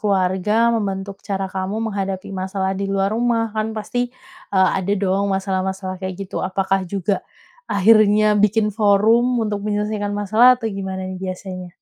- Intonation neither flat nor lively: No, narrow, 2.0 semitones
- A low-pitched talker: No, high, 200 Hz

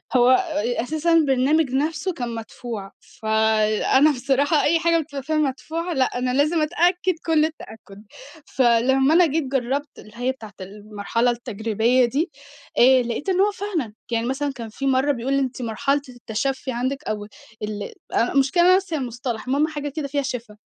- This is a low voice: No, very high, 265 Hz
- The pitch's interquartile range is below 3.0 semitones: No, average, 4.5 semitones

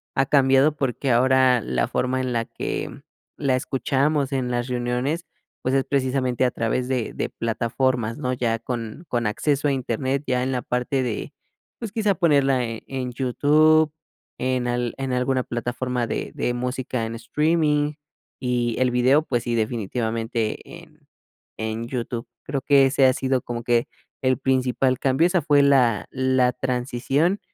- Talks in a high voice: No, low, 130 Hz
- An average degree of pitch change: No, narrow, 2.1 semitones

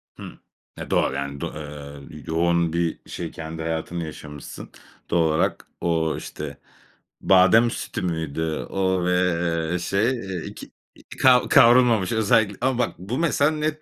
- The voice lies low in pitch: Yes, very low, 90 Hz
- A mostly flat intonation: No, wide, 6.1 semitones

